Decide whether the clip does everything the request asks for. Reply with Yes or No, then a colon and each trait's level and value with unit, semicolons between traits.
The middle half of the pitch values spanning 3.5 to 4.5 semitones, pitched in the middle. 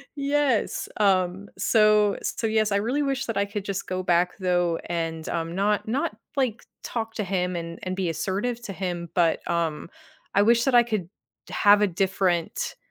No: average, 3.9 semitones; high, 195 Hz